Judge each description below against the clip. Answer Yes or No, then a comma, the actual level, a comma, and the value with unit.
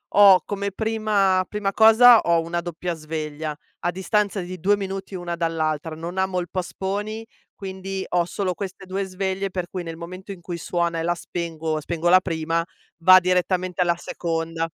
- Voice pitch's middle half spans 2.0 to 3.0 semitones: Yes, narrow, 2.5 semitones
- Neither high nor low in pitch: Yes, medium, 180 Hz